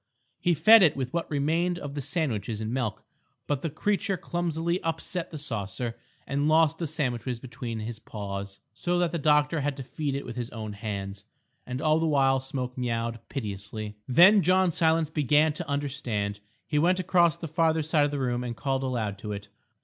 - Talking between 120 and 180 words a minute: No, average, 195 wpm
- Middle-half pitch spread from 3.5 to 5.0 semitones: No, wide, 5.6 semitones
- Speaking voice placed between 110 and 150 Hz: Yes, medium, 140 Hz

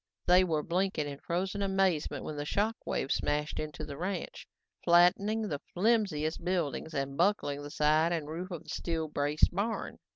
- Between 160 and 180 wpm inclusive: Yes, average, 170 wpm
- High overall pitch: No, medium, 170 Hz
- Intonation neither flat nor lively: Yes, average, 4.2 semitones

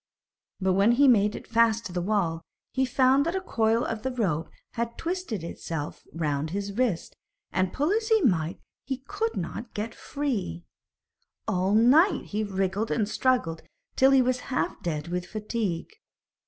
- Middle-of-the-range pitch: No, high, 220 Hz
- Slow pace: No, average, 170 wpm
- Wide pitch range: Yes, wide, 6.0 semitones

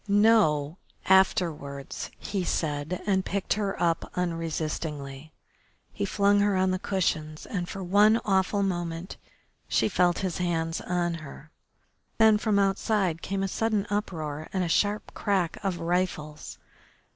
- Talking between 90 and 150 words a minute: Yes, slow, 135 wpm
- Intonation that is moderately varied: Yes, average, 3.5 semitones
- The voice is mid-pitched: Yes, medium, 180 Hz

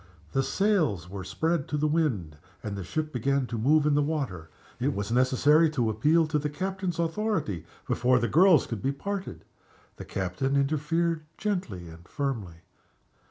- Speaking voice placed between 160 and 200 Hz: No, medium, 140 Hz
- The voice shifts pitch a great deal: Yes, wide, 7.3 semitones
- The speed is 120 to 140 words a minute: No, average, 165 wpm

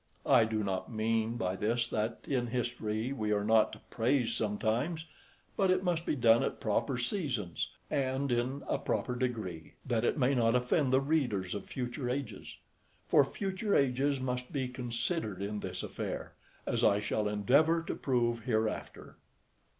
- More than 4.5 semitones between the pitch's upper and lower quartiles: No, average, 3.9 semitones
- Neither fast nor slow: Yes, average, 165 wpm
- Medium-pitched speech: No, low, 120 Hz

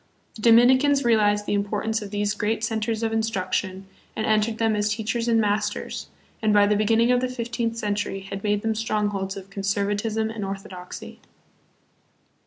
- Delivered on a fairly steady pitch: Yes, narrow, 1.7 semitones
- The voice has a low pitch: No, high, 215 Hz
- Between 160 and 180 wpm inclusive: Yes, average, 170 wpm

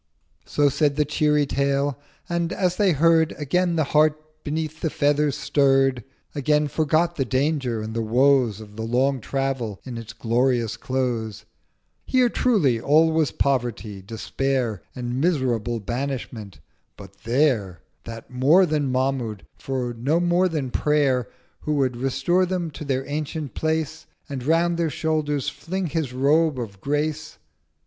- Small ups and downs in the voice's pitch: No, average, 4.2 semitones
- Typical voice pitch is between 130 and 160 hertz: Yes, medium, 140 Hz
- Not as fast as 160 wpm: Yes, average, 145 wpm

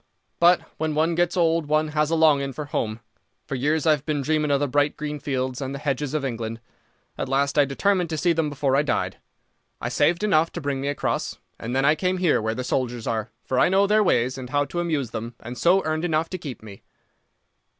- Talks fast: Yes, fast, 235 wpm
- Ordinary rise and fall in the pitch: Yes, average, 3.6 semitones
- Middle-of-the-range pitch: Yes, medium, 145 Hz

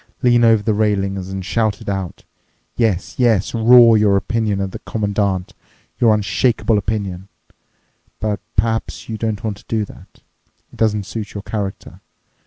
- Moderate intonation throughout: No, narrow, 2.3 semitones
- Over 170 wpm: No, average, 150 wpm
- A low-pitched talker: Yes, low, 105 Hz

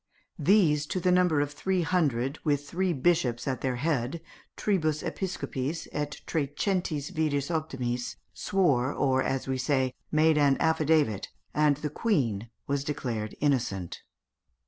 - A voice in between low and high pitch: Yes, medium, 145 Hz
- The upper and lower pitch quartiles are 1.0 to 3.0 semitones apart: No, average, 3.6 semitones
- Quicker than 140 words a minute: No, slow, 135 wpm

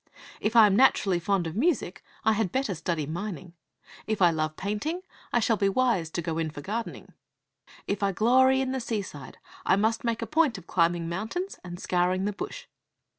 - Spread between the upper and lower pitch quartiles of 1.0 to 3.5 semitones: No, average, 5.1 semitones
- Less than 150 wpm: No, average, 195 wpm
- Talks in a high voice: Yes, high, 200 Hz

